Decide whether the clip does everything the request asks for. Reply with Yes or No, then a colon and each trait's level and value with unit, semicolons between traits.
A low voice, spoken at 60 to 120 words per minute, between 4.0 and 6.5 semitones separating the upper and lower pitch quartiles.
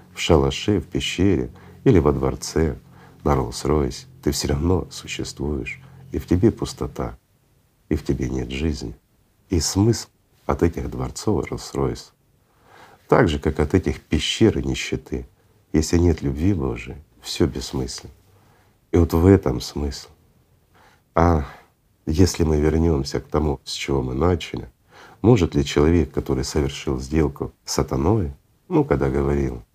No: very low, 75 Hz; average, 135 wpm; average, 4.3 semitones